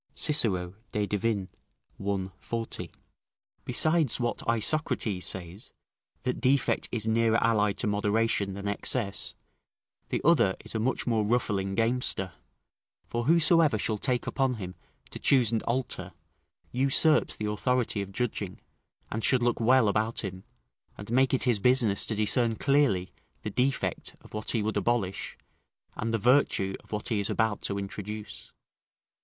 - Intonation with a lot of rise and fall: No, average, 3.6 semitones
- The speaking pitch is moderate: No, low, 110 Hz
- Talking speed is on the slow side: No, average, 150 wpm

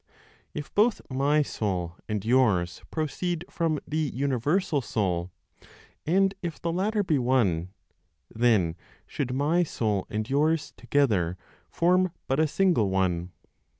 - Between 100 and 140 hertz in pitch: Yes, low, 135 Hz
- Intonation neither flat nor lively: No, wide, 8.1 semitones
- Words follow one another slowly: Yes, slow, 125 wpm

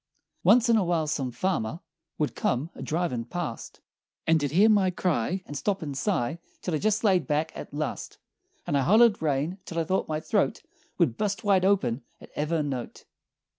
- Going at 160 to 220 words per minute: Yes, average, 190 wpm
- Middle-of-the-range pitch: Yes, medium, 165 Hz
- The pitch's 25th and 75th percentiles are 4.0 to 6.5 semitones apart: Yes, average, 4.9 semitones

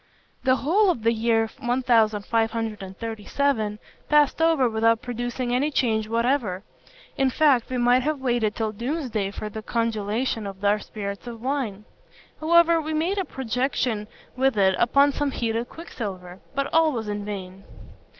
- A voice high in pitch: Yes, high, 235 Hz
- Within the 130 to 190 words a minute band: Yes, average, 150 wpm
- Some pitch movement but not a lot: Yes, average, 4.0 semitones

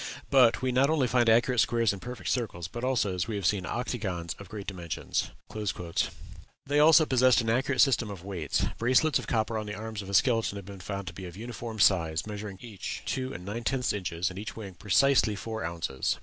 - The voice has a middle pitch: No, low, 110 Hz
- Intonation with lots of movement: No, average, 4.4 semitones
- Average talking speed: No, fast, 215 wpm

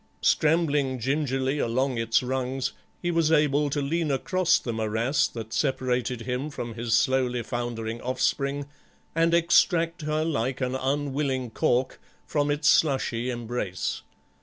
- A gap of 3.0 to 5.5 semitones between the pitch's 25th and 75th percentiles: Yes, average, 3.5 semitones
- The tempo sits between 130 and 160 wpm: Yes, slow, 135 wpm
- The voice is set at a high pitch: No, low, 130 Hz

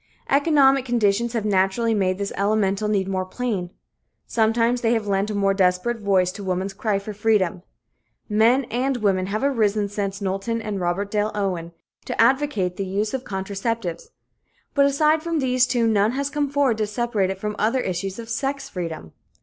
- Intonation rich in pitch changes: No, average, 3.7 semitones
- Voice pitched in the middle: No, high, 210 Hz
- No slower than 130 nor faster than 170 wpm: No, average, 180 wpm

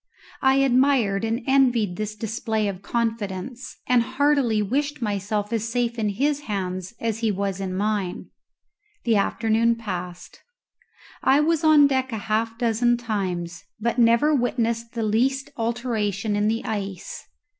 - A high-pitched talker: Yes, high, 225 Hz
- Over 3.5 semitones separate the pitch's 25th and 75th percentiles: No, average, 3.2 semitones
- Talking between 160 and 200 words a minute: No, average, 145 wpm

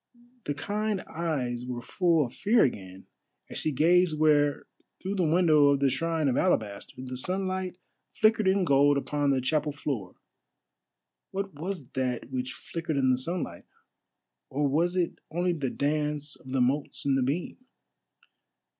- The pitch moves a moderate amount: Yes, average, 4.9 semitones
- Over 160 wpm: No, average, 155 wpm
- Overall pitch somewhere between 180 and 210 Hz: No, medium, 150 Hz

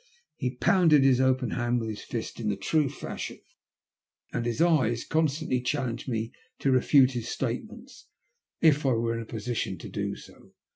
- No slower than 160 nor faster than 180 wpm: Yes, average, 175 wpm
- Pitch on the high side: No, low, 125 Hz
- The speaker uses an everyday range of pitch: Yes, average, 3.1 semitones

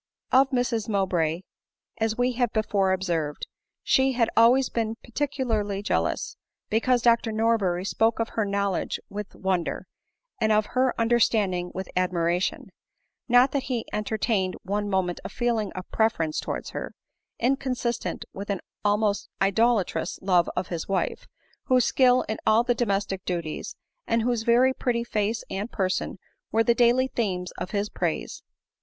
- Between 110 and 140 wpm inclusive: No, average, 150 wpm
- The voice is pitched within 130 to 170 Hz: No, high, 220 Hz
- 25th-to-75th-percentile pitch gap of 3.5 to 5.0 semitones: Yes, average, 3.8 semitones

